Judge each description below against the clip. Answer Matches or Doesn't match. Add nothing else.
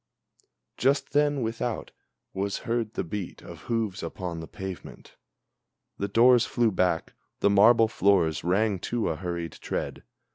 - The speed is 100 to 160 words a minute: Matches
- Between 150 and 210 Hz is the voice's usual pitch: Doesn't match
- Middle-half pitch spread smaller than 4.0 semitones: Doesn't match